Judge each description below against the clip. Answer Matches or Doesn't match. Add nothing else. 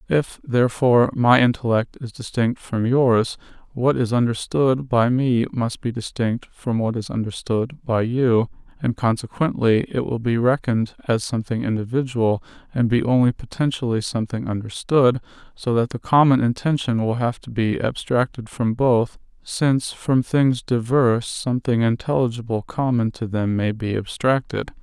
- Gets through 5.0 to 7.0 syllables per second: Doesn't match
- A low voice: Matches